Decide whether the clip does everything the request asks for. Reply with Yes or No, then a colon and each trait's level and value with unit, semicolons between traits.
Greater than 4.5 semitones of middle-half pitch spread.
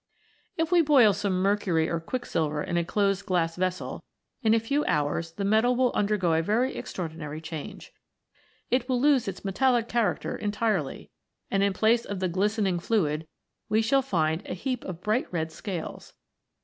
Yes: wide, 5.4 semitones